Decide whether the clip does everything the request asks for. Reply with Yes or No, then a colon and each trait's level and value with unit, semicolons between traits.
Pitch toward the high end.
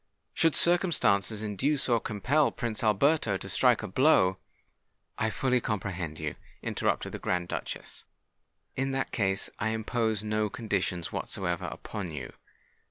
No: low, 110 Hz